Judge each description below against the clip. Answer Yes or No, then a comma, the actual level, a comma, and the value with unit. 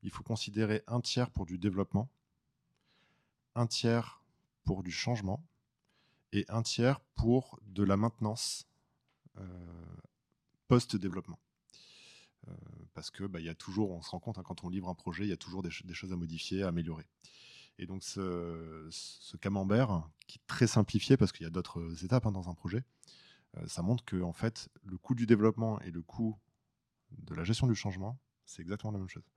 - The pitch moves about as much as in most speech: Yes, average, 4.7 semitones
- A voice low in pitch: Yes, low, 105 Hz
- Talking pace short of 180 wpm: No, average, 190 wpm